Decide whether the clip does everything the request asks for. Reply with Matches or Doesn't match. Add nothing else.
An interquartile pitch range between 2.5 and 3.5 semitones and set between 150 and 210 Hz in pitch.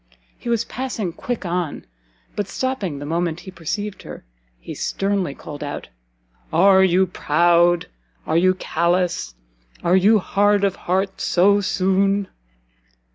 Matches